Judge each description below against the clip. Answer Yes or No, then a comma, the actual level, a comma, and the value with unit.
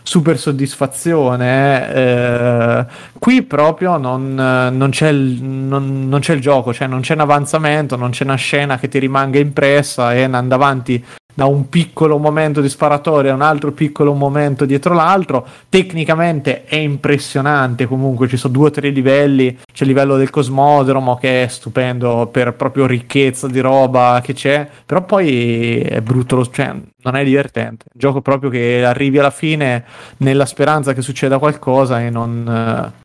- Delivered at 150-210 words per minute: Yes, fast, 170 wpm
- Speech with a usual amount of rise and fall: No, narrow, 2.3 semitones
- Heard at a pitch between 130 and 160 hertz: Yes, low, 135 Hz